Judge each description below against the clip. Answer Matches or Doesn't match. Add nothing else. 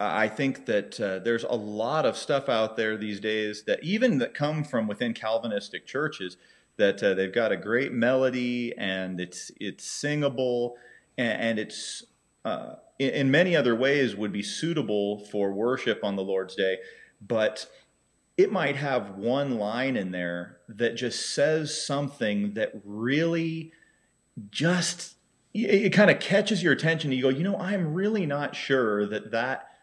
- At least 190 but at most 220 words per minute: Doesn't match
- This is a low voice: Matches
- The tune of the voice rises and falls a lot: Matches